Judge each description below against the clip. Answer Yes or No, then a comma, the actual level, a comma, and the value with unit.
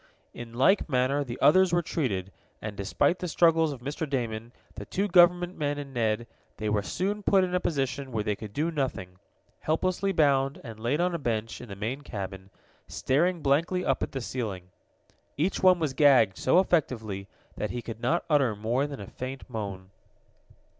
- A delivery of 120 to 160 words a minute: No, average, 190 wpm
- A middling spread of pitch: No, wide, 6.9 semitones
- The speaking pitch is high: No, low, 135 Hz